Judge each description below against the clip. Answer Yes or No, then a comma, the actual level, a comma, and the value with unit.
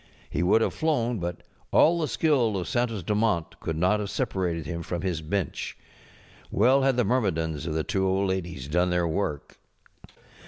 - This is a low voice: Yes, very low, 95 Hz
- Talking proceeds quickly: No, average, 180 wpm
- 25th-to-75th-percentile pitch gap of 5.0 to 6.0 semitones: Yes, average, 5.3 semitones